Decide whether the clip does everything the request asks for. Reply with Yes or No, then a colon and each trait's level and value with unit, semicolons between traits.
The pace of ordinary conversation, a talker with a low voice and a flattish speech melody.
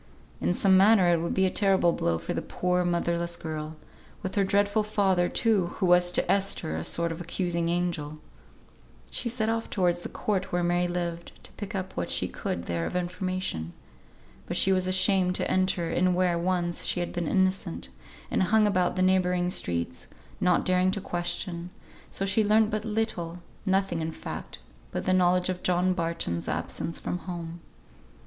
No: average, 185 wpm; medium, 180 Hz; narrow, 1.9 semitones